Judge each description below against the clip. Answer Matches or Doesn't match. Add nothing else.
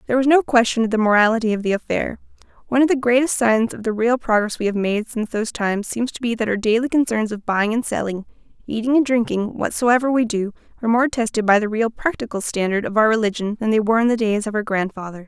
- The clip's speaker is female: Matches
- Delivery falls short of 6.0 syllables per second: Doesn't match